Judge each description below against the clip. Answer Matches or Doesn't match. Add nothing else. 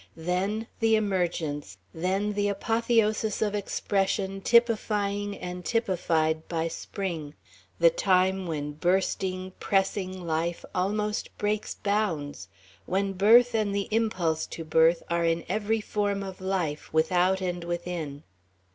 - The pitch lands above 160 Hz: Matches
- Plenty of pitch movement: Doesn't match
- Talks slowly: Matches